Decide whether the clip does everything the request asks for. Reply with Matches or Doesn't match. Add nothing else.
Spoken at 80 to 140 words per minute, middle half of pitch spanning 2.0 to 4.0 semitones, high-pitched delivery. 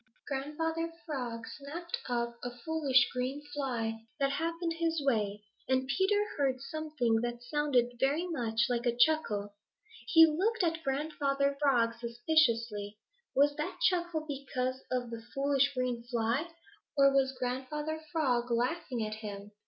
Doesn't match